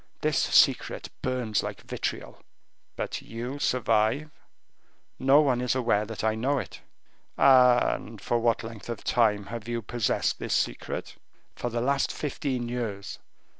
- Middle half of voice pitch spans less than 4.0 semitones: Yes, narrow, 2.5 semitones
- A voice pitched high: No, low, 120 Hz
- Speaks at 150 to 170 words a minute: No, average, 140 wpm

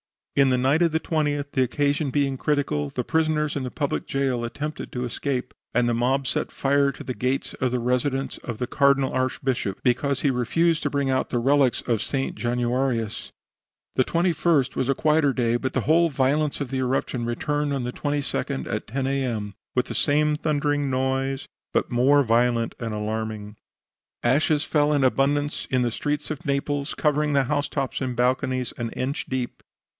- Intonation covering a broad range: No, average, 2.8 semitones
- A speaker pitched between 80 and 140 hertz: Yes, low, 135 Hz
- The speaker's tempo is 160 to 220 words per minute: Yes, average, 185 wpm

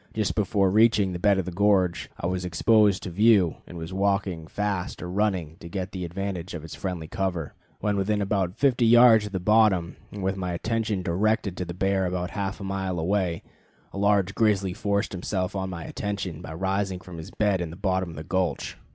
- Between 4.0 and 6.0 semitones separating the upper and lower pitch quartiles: No, narrow, 2.5 semitones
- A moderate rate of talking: No, fast, 210 wpm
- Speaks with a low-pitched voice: Yes, very low, 95 Hz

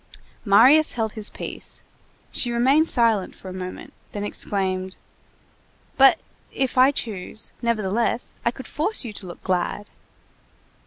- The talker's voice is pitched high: Yes, high, 225 Hz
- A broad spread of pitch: No, average, 4.8 semitones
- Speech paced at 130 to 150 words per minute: Yes, slow, 135 wpm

